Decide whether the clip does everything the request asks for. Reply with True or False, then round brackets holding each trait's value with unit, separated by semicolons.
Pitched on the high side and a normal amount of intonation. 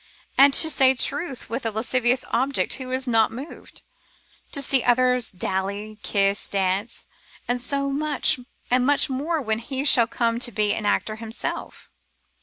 True (245 Hz; 3.4 semitones)